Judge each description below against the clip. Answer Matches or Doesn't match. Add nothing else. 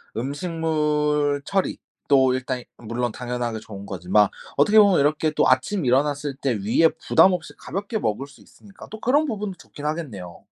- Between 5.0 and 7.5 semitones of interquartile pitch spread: Matches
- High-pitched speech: Doesn't match